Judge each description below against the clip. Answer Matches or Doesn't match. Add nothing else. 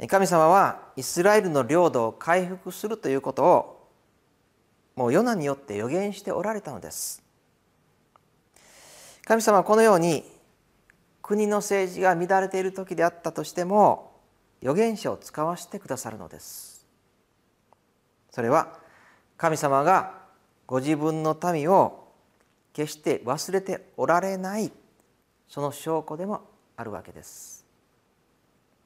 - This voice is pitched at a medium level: Matches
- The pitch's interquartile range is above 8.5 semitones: Doesn't match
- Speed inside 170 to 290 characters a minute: Matches